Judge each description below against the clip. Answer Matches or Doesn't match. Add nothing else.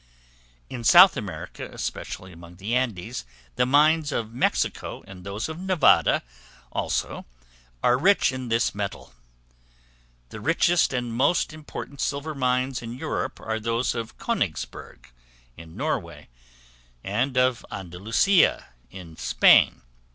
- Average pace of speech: Doesn't match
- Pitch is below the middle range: Matches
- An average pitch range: Doesn't match